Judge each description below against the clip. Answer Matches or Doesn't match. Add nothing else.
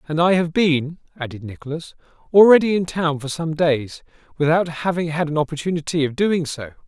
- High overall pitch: Doesn't match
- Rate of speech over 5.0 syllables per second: Matches